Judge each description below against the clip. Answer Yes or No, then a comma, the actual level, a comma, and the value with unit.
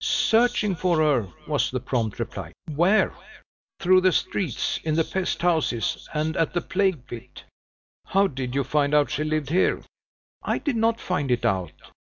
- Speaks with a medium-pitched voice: Yes, medium, 160 Hz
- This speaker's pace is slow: No, average, 170 wpm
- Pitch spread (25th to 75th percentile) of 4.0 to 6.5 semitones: Yes, average, 5.3 semitones